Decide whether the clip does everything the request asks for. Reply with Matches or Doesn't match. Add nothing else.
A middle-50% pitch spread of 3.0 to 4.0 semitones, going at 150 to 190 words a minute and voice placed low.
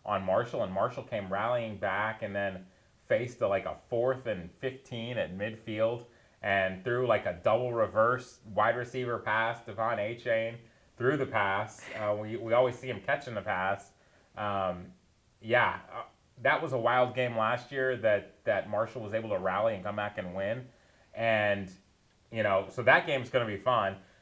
Matches